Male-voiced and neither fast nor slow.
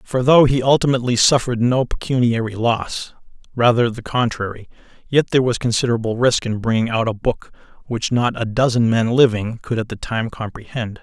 Yes: male; average, 175 wpm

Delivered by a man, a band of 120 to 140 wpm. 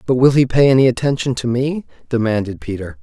No: male; average, 200 wpm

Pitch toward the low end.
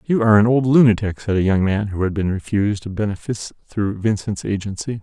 Yes: low, 105 Hz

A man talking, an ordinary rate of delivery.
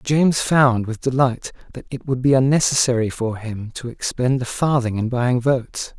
Yes: male; average, 180 wpm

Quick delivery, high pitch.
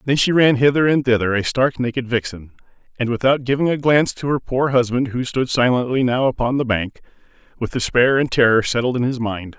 No: fast, 215 wpm; low, 125 Hz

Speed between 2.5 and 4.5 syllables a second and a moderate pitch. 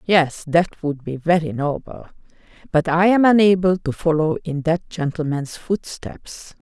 Yes: 4.2 syllables/s; medium, 165 Hz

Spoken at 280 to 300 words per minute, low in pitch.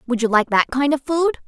No: fast, 285 wpm; very high, 265 Hz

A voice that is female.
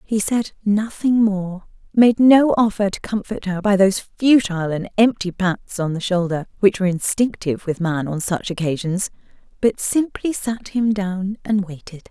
Yes: female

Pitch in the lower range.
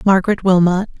No: high, 190 Hz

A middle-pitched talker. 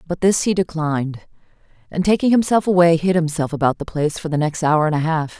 Yes: medium, 165 Hz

